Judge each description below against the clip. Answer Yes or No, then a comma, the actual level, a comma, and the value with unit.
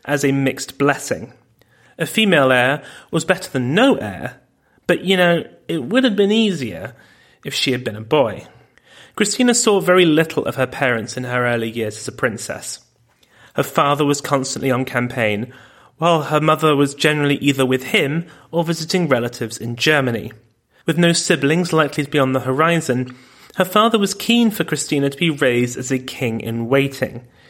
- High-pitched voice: No, medium, 140 Hz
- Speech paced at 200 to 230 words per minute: No, average, 180 wpm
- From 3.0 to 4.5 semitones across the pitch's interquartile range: No, average, 5.0 semitones